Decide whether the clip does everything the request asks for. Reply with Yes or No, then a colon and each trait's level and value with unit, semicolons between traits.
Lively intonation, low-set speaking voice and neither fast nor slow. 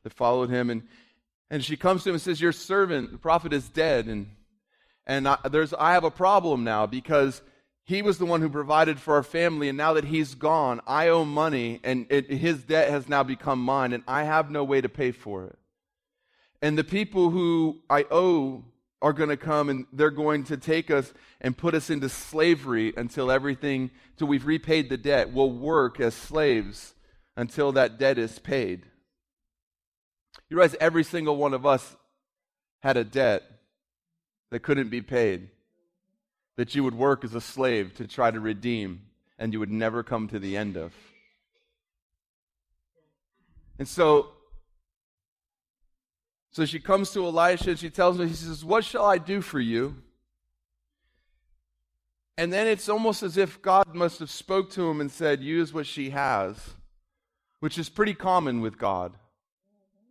No: wide, 5.7 semitones; medium, 145 Hz; average, 175 wpm